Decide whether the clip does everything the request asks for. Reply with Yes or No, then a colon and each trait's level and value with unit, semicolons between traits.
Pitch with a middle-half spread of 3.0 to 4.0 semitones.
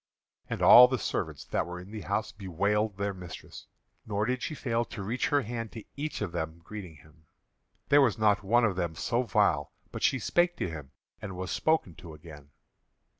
No: average, 5.1 semitones